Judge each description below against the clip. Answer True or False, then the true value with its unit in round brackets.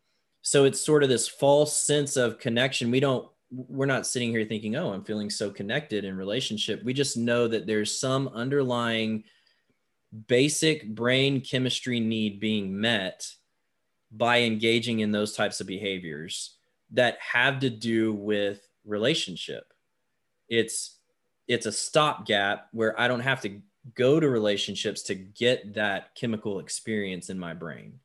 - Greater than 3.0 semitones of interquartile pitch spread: True (3.4 semitones)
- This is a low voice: True (115 Hz)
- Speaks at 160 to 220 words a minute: False (150 wpm)